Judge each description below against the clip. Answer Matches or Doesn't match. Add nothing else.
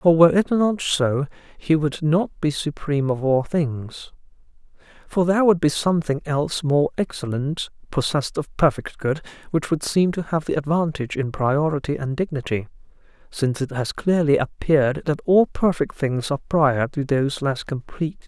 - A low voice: Doesn't match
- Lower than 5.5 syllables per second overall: Matches